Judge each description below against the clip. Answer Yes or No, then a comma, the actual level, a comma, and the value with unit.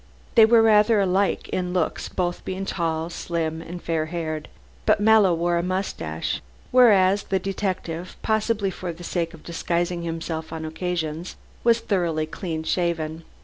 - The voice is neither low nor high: Yes, medium, 175 Hz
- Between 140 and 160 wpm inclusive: Yes, average, 145 wpm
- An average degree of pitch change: Yes, average, 3.0 semitones